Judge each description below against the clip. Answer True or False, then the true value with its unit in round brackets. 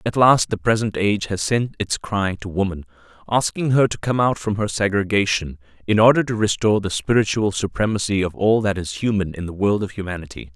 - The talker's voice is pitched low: True (100 Hz)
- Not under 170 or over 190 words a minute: False (205 wpm)